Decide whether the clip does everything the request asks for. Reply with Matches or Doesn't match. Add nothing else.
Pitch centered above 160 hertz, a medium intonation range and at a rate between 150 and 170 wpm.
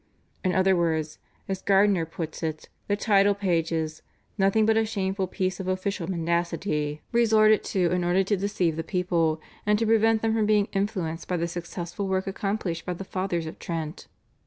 Doesn't match